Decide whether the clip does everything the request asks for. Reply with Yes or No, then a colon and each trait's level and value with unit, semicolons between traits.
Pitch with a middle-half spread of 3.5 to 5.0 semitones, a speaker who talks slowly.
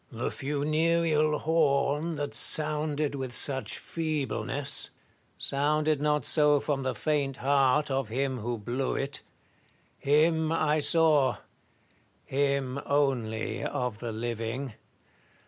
No: narrow, 2.6 semitones; slow, 110 wpm